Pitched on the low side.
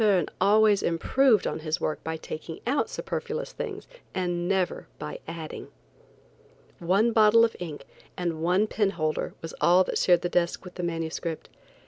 No: medium, 180 Hz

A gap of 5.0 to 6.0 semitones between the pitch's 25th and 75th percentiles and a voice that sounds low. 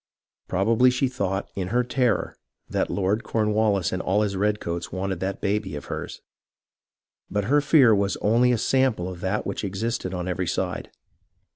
No: average, 3.7 semitones; low, 100 Hz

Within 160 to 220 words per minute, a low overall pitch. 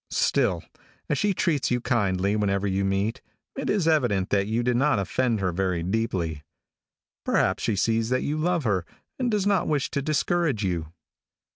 Yes: average, 175 wpm; low, 115 Hz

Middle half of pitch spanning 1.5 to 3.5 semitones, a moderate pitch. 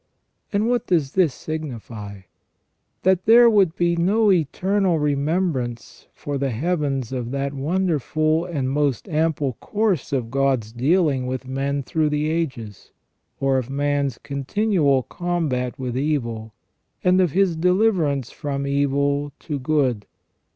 No: average, 4.7 semitones; medium, 145 Hz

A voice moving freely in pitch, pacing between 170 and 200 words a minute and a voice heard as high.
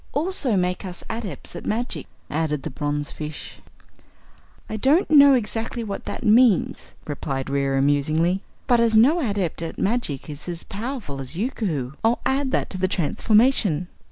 No: wide, 7.9 semitones; average, 155 wpm; high, 195 Hz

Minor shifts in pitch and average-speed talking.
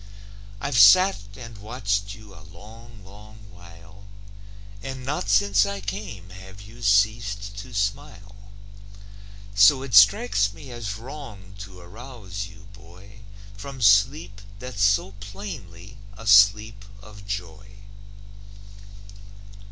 No: narrow, 2.3 semitones; slow, 115 wpm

